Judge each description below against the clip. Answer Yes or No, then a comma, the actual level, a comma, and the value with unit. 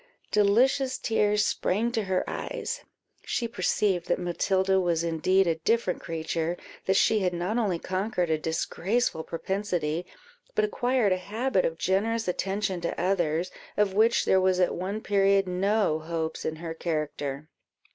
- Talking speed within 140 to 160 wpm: Yes, average, 150 wpm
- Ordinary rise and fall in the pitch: Yes, average, 3.7 semitones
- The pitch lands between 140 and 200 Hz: Yes, high, 190 Hz